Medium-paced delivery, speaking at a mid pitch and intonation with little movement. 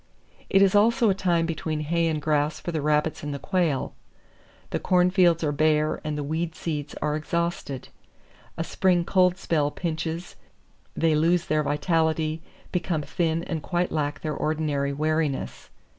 Yes: average, 160 wpm; medium, 160 Hz; narrow, 2.3 semitones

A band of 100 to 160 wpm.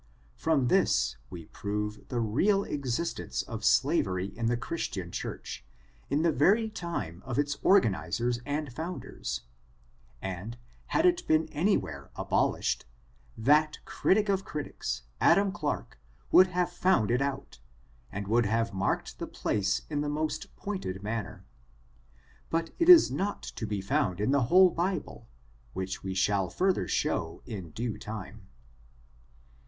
Yes: average, 140 wpm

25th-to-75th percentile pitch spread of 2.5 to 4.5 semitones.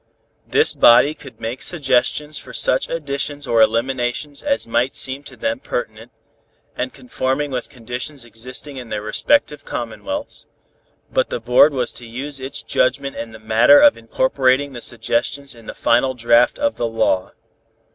Yes: average, 3.6 semitones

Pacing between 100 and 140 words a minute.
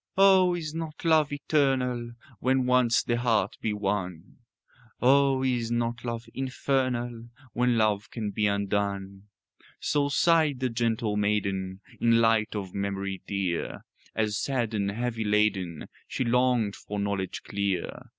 Yes: slow, 135 wpm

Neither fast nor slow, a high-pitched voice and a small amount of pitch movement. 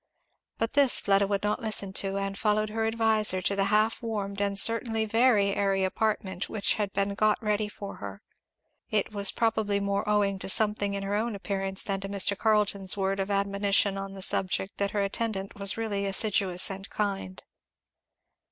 Yes: average, 180 wpm; high, 200 Hz; narrow, 1.5 semitones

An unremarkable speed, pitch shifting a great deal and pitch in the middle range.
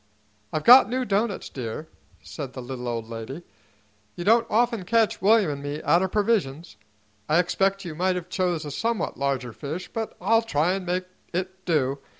Yes: average, 180 wpm; wide, 6.4 semitones; medium, 180 Hz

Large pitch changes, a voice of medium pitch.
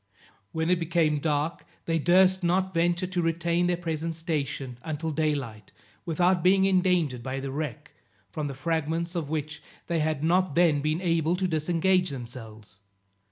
No: average, 3.0 semitones; medium, 165 Hz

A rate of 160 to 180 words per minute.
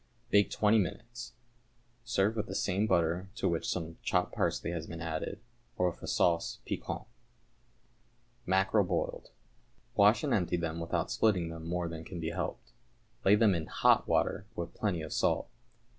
Yes: average, 170 wpm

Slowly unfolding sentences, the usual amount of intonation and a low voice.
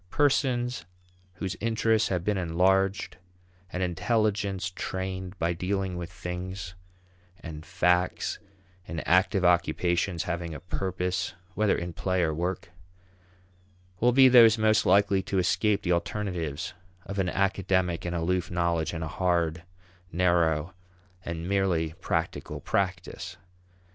No: slow, 125 wpm; narrow, 2.3 semitones; very low, 90 Hz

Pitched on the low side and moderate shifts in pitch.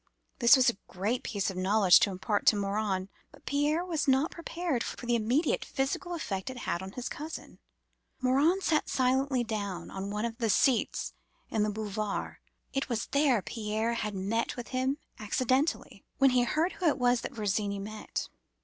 No: high, 235 Hz; average, 4.5 semitones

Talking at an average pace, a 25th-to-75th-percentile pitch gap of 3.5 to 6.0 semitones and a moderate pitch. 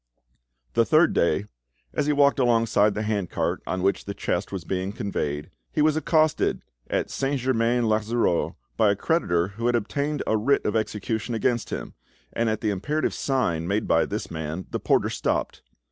No: average, 175 wpm; average, 4.8 semitones; low, 110 Hz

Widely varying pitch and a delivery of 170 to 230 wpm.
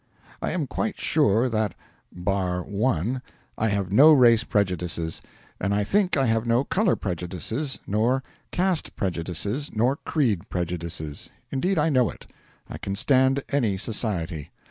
No: wide, 6.5 semitones; average, 145 wpm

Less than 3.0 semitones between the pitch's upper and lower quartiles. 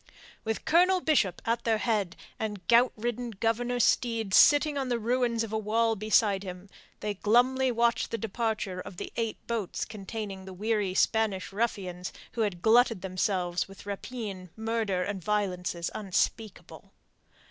No: average, 3.3 semitones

